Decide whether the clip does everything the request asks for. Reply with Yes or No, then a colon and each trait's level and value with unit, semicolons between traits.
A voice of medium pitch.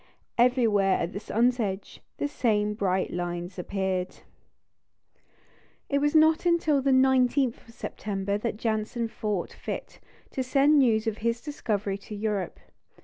No: high, 220 Hz